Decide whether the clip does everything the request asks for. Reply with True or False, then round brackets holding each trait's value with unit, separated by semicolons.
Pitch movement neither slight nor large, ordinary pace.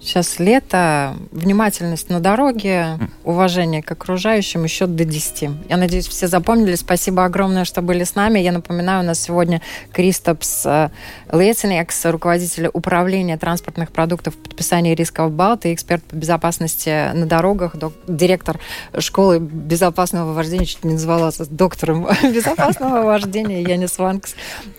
False (2.1 semitones; 135 wpm)